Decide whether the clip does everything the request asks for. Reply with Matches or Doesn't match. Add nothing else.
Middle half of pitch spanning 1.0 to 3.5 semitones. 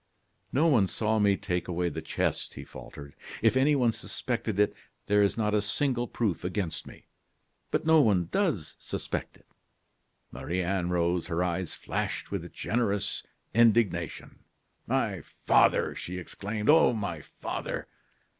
Doesn't match